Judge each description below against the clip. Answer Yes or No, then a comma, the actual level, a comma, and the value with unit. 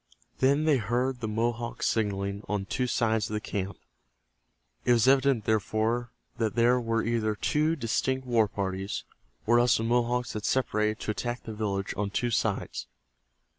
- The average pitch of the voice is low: Yes, low, 115 Hz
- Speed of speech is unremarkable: Yes, average, 165 wpm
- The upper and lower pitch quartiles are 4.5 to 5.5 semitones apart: No, narrow, 2.5 semitones